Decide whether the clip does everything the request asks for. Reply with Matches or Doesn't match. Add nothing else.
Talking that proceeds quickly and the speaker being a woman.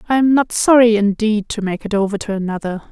Matches